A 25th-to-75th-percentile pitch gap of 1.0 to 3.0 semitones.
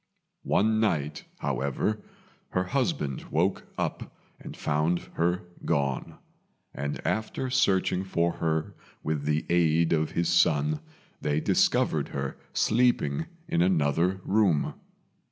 No: average, 4.1 semitones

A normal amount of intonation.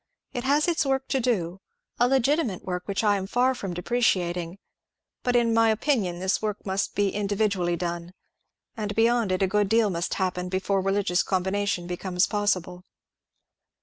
Yes: average, 4.1 semitones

